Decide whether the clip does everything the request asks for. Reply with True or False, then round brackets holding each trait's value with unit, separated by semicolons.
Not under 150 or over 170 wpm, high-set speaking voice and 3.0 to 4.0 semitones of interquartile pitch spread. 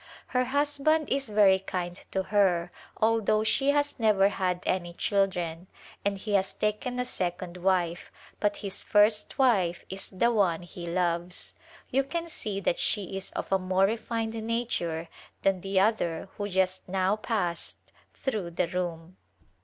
True (155 wpm; 195 Hz; 3.6 semitones)